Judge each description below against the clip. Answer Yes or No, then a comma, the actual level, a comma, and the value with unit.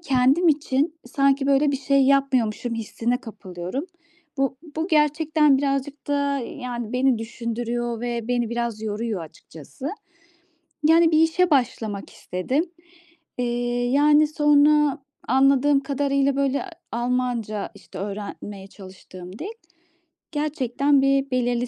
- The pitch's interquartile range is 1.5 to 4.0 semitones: Yes, average, 3.5 semitones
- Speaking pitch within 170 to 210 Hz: No, very high, 265 Hz